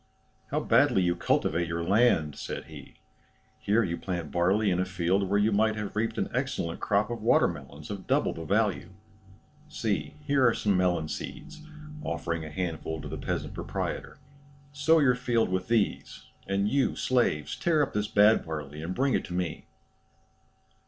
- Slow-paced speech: No, average, 175 wpm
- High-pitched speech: No, low, 100 Hz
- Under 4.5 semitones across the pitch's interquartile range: No, average, 5.1 semitones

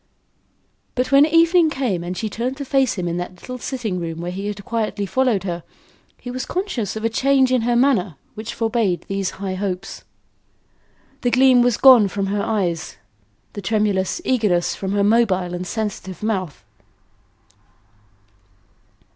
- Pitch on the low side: No, high, 215 Hz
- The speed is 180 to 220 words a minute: No, average, 160 wpm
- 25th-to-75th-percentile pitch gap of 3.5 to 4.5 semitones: No, average, 5.1 semitones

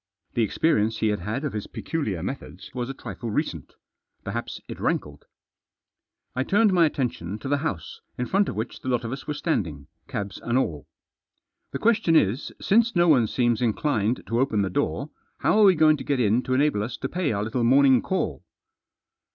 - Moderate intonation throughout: No, wide, 6.0 semitones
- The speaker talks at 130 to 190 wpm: No, average, 200 wpm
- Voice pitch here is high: No, low, 125 Hz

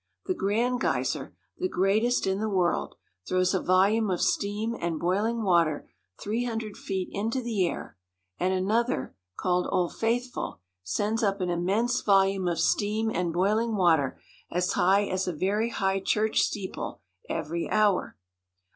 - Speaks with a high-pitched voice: Yes, high, 195 Hz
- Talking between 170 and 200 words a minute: No, average, 155 wpm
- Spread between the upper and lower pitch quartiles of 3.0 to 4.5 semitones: Yes, average, 3.5 semitones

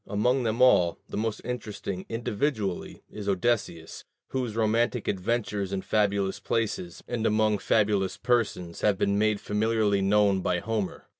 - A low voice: Yes, low, 105 Hz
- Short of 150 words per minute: Yes, average, 140 wpm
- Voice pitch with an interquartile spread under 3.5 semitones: Yes, narrow, 2.5 semitones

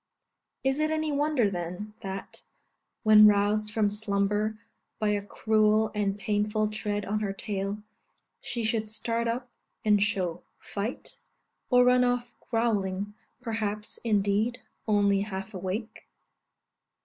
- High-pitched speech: Yes, high, 210 Hz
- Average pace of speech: No, slow, 125 wpm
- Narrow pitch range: Yes, narrow, 2.1 semitones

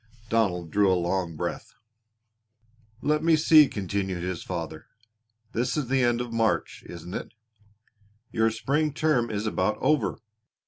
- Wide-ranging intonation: Yes, wide, 6.4 semitones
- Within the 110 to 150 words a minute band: Yes, average, 140 wpm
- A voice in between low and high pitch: No, low, 110 Hz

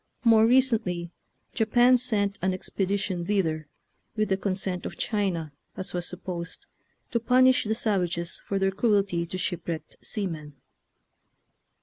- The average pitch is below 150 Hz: No, high, 195 Hz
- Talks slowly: Yes, slow, 125 wpm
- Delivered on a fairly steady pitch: No, average, 3.8 semitones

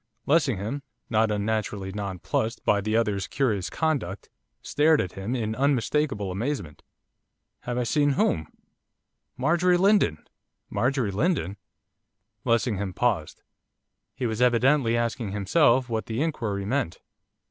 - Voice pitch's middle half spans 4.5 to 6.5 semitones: Yes, average, 5.2 semitones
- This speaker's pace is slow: Yes, slow, 115 wpm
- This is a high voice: No, low, 115 Hz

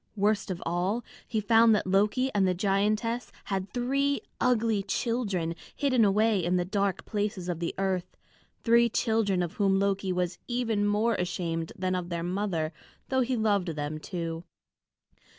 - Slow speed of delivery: No, average, 160 wpm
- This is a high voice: Yes, high, 200 Hz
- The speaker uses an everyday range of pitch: Yes, average, 3.9 semitones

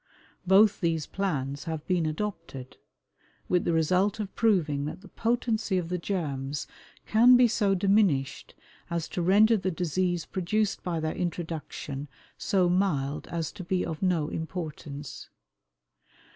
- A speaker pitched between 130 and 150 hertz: No, medium, 175 Hz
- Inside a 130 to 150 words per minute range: Yes, average, 140 wpm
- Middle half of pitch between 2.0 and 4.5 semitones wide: Yes, average, 4.0 semitones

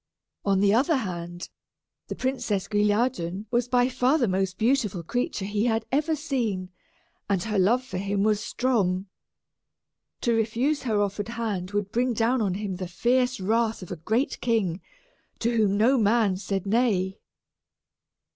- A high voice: Yes, high, 215 Hz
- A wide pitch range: No, average, 4.1 semitones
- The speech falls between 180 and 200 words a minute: No, average, 155 wpm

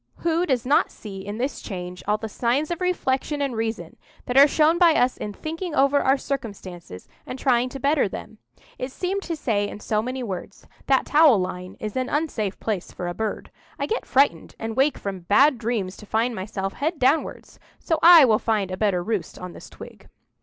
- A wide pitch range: Yes, wide, 5.9 semitones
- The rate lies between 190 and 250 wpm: Yes, fast, 205 wpm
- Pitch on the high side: Yes, high, 245 Hz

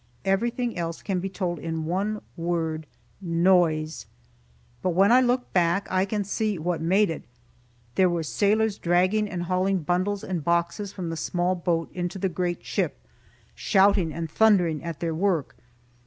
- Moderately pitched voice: Yes, medium, 180 Hz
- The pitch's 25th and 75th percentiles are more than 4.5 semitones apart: No, average, 2.9 semitones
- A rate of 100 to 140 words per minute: No, average, 160 wpm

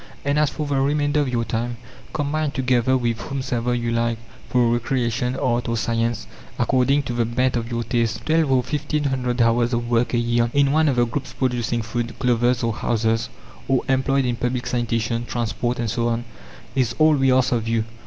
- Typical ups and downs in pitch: No, narrow, 2.1 semitones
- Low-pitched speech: Yes, low, 120 Hz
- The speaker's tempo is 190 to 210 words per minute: Yes, average, 200 wpm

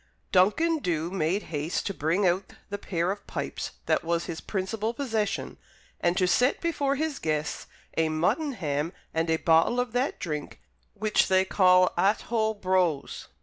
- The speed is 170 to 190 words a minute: No, average, 155 wpm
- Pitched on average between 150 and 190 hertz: Yes, medium, 185 Hz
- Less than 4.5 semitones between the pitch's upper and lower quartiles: No, average, 4.9 semitones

